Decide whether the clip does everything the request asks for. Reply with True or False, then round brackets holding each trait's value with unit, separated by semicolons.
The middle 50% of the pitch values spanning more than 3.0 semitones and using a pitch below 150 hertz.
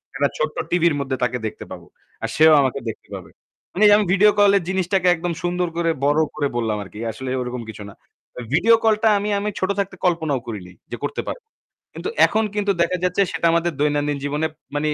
False (5.3 semitones; 165 Hz)